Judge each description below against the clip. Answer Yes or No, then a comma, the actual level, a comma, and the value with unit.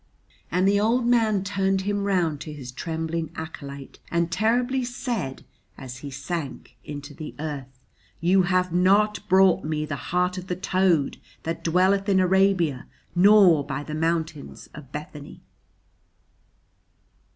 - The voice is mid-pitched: Yes, medium, 175 Hz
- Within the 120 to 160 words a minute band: Yes, average, 140 wpm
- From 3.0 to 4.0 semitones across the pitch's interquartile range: No, average, 4.4 semitones